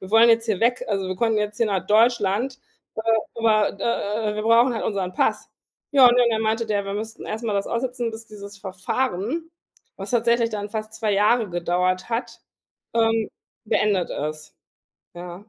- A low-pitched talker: No, high, 220 Hz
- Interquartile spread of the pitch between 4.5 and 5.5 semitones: No, narrow, 2.6 semitones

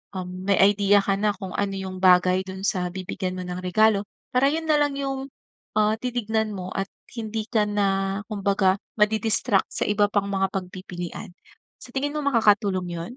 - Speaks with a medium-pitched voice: No, high, 200 Hz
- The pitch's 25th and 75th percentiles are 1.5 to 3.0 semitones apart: Yes, average, 2.7 semitones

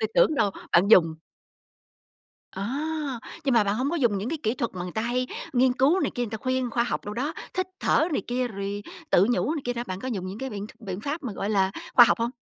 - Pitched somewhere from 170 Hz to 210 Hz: No, high, 235 Hz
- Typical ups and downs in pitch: Yes, average, 4.6 semitones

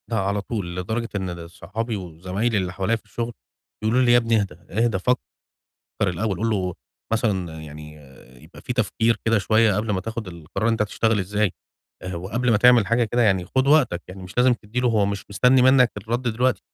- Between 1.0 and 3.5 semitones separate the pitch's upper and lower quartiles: No, average, 3.9 semitones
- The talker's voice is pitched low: Yes, low, 105 Hz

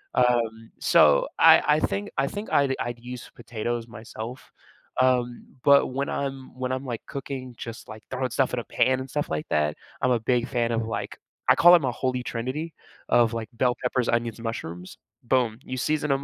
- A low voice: Yes, low, 125 Hz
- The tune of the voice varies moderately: No, narrow, 2.3 semitones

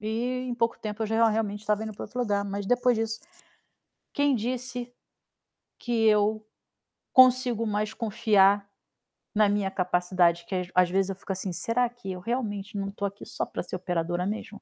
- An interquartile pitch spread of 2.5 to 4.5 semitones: Yes, average, 2.9 semitones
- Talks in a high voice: Yes, high, 210 Hz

